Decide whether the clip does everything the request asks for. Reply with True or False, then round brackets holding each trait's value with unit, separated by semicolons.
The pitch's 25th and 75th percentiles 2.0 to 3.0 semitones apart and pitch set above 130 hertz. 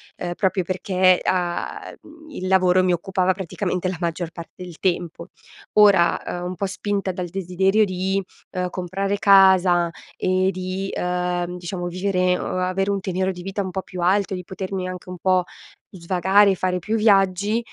False (1.4 semitones; 185 Hz)